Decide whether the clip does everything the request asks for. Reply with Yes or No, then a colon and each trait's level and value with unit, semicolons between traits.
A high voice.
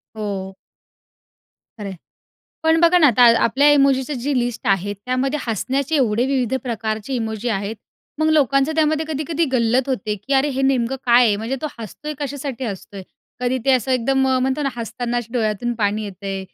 Yes: very high, 250 Hz